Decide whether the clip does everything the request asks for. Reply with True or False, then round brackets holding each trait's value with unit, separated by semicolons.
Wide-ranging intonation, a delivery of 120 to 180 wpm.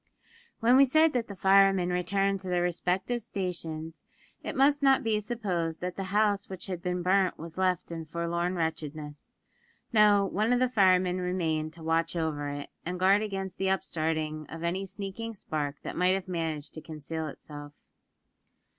False (3.3 semitones; 170 wpm)